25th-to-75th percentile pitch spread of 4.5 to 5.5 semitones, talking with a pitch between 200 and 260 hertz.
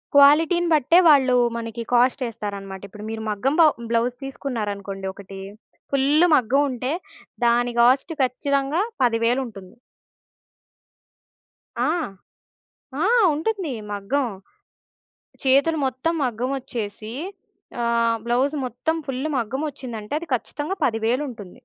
No: average, 3.7 semitones; very high, 250 Hz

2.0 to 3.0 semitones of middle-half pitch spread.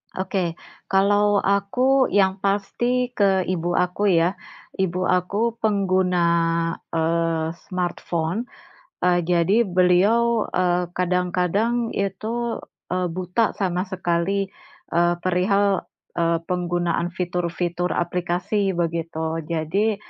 Yes: narrow, 2.5 semitones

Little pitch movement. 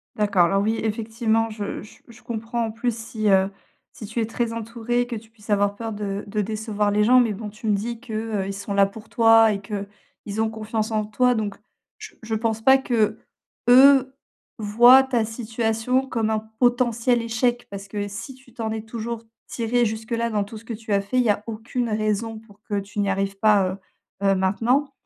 Yes: narrow, 2.1 semitones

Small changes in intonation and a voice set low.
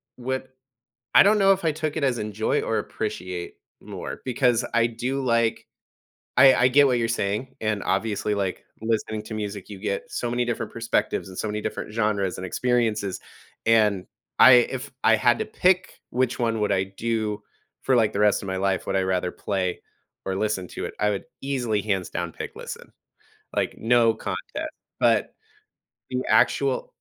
No: average, 3.7 semitones; low, 110 Hz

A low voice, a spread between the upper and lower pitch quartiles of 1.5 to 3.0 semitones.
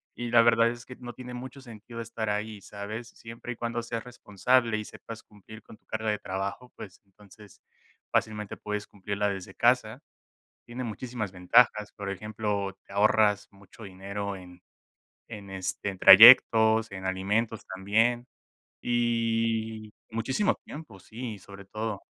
Yes: low, 110 Hz; narrow, 2.6 semitones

